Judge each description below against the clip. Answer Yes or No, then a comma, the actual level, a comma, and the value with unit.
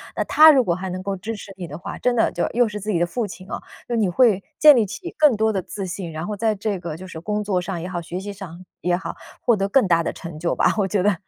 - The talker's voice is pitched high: Yes, high, 195 Hz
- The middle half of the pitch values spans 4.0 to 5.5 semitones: No, average, 3.4 semitones